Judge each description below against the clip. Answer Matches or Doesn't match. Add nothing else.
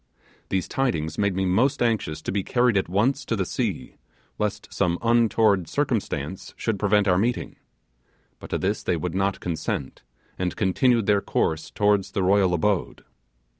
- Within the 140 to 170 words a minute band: Matches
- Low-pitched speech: Matches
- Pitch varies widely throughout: Doesn't match